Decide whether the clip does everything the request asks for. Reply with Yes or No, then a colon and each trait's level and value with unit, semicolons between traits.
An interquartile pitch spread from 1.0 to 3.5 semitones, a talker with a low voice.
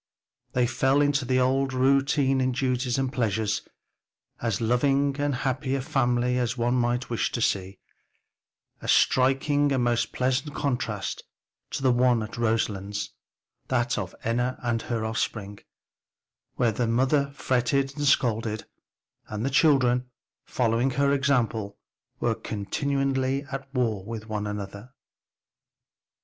Yes: average, 3.1 semitones; low, 125 Hz